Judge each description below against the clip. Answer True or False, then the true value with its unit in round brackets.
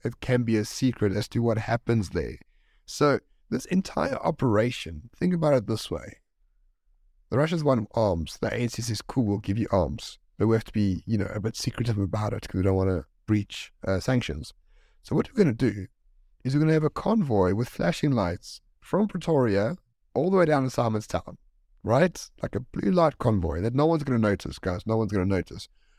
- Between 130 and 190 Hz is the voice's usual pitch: False (110 Hz)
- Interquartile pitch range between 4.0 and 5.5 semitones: True (4.7 semitones)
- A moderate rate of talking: False (215 wpm)